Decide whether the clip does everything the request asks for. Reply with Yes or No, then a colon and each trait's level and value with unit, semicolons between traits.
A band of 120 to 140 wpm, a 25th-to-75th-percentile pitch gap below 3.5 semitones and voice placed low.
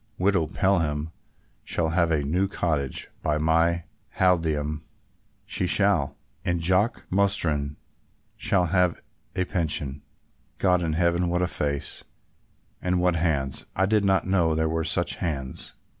Yes: slow, 135 wpm; average, 3.0 semitones; very low, 85 Hz